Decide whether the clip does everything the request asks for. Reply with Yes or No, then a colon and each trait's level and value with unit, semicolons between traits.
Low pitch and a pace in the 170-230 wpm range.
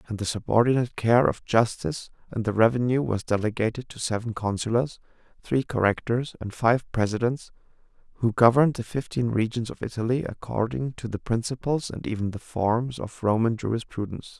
No: low, 115 Hz; average, 155 wpm